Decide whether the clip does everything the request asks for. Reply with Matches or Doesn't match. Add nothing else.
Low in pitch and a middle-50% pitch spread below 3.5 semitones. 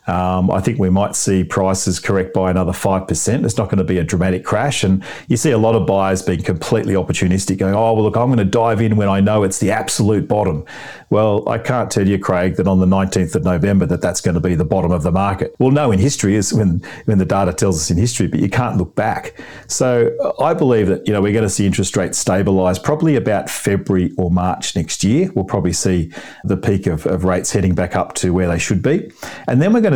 Matches